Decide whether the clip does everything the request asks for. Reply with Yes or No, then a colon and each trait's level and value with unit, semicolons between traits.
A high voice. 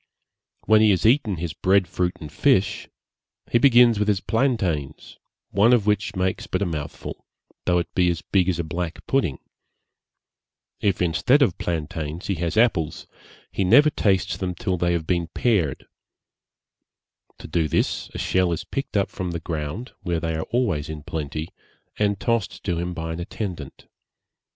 No: very low, 90 Hz